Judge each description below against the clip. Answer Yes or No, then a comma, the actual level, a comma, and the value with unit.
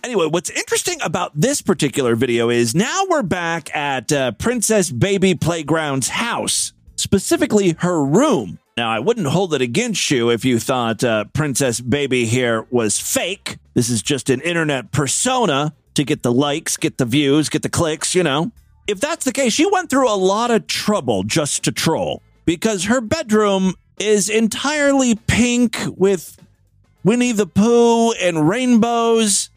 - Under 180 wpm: Yes, average, 160 wpm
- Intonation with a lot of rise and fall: Yes, wide, 8.8 semitones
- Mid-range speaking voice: Yes, medium, 170 Hz